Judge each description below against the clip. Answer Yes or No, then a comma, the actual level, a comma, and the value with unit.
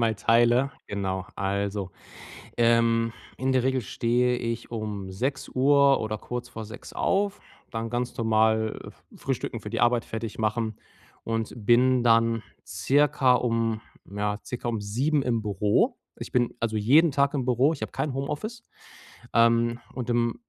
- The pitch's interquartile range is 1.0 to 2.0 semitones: No, narrow, 2.6 semitones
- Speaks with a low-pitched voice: Yes, low, 115 Hz